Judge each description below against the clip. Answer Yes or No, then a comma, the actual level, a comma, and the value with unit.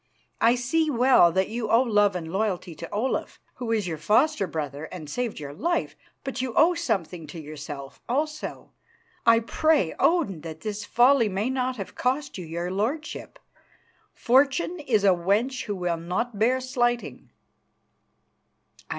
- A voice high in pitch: Yes, high, 225 Hz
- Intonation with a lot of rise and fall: Yes, wide, 6.5 semitones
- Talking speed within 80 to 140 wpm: No, average, 155 wpm